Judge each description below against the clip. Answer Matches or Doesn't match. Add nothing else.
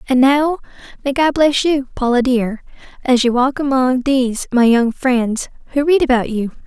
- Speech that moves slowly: Doesn't match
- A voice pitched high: Matches